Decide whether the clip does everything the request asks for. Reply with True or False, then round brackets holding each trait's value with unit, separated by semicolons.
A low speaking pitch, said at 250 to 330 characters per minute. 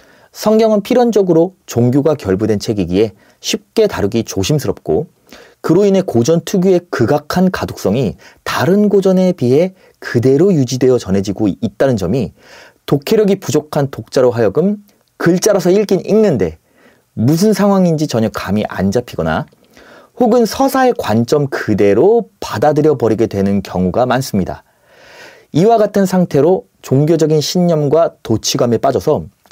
False (155 Hz; 305 characters per minute)